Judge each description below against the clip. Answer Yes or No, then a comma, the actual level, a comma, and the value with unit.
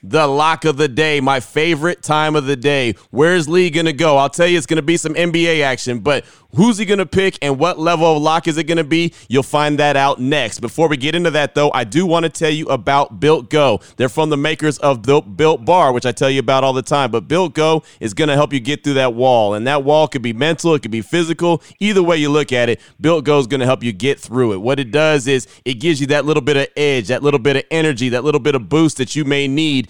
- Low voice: No, medium, 150 Hz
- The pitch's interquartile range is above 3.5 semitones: No, average, 2.8 semitones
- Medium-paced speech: No, fast, 270 wpm